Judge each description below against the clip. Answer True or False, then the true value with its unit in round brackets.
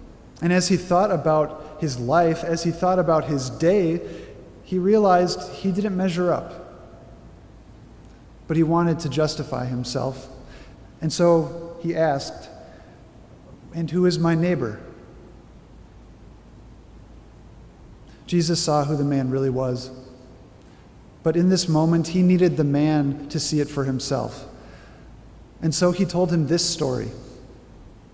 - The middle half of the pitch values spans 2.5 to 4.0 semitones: False (4.9 semitones)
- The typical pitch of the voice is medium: True (155 Hz)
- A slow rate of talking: True (130 wpm)